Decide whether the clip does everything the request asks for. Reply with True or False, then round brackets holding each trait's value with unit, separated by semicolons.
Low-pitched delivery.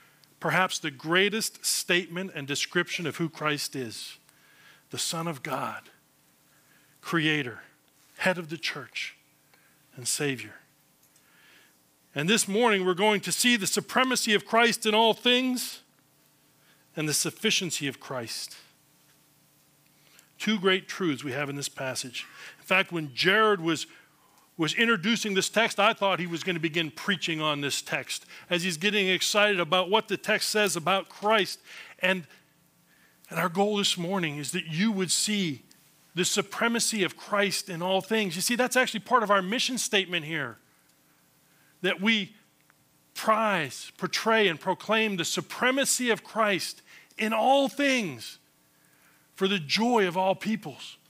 False (185 Hz)